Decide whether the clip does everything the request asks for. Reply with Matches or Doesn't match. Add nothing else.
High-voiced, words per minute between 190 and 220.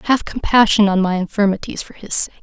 Matches